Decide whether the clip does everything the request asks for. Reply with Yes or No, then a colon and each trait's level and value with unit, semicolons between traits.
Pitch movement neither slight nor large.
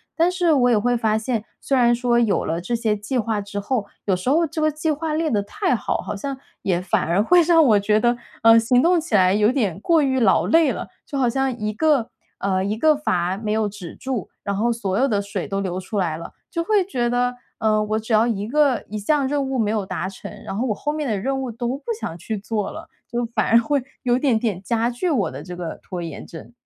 Yes: average, 4.9 semitones